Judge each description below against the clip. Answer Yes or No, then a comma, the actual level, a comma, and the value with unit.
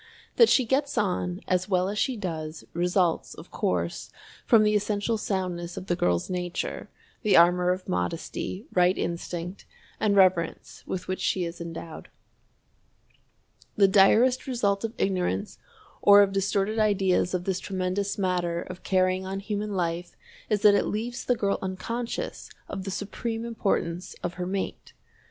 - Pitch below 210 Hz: Yes, high, 190 Hz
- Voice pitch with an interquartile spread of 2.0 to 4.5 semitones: Yes, average, 2.7 semitones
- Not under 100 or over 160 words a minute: Yes, average, 155 wpm